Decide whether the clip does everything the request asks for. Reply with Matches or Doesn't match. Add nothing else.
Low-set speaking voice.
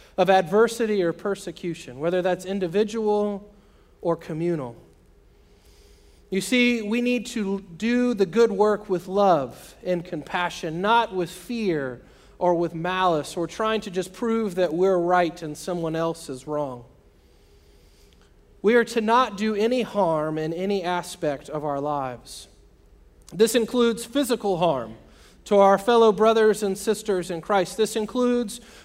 Doesn't match